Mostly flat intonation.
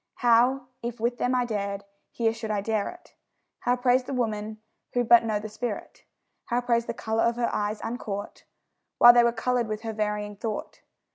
Yes: narrow, 2.2 semitones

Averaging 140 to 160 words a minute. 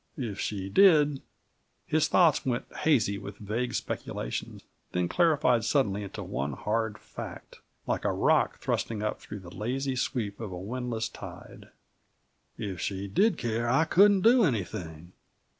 Yes: average, 150 wpm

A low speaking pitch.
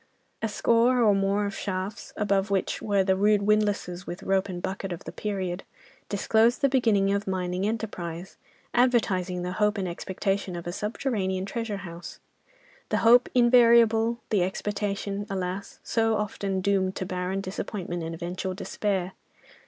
No: high, 200 Hz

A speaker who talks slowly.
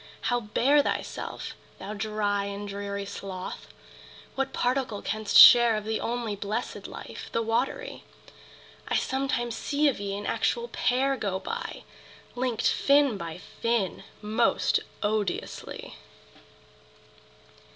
Yes: slow, 120 wpm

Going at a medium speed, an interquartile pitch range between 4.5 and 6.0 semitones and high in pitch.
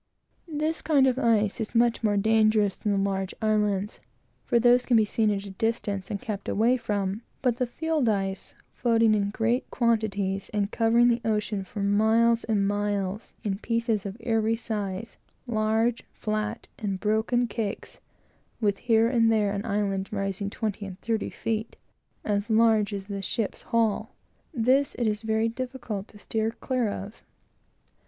No: average, 165 wpm; narrow, 2.4 semitones; high, 220 Hz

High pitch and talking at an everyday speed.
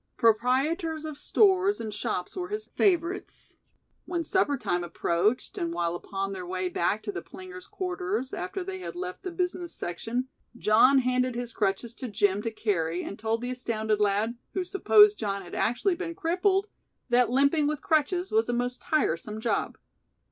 Yes: very high, 250 Hz; average, 170 wpm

